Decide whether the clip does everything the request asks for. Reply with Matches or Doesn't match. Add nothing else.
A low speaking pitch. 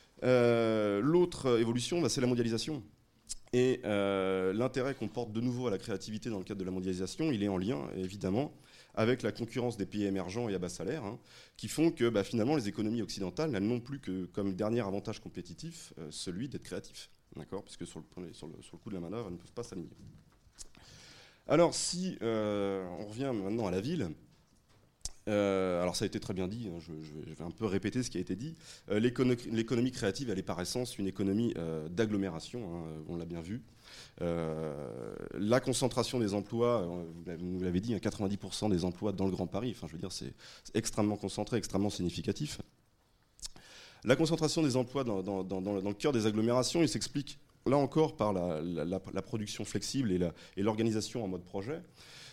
Matches